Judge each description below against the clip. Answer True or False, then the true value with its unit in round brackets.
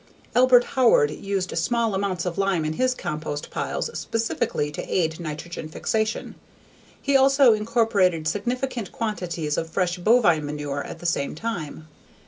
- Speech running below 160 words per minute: True (140 wpm)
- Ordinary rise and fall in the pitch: False (6.3 semitones)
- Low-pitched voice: False (185 Hz)